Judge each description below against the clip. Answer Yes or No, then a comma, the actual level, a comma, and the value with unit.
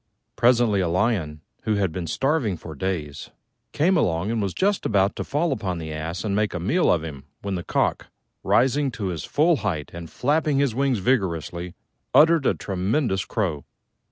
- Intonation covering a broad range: Yes, wide, 7.6 semitones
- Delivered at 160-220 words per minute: Yes, average, 185 wpm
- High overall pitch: No, low, 100 Hz